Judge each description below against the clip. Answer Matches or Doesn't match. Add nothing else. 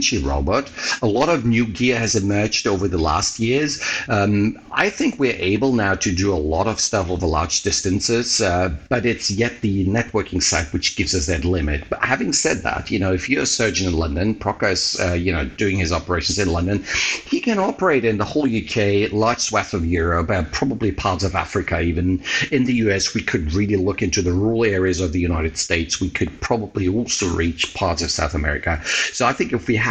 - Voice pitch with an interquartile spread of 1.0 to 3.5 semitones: Doesn't match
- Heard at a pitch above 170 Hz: Doesn't match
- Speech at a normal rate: Doesn't match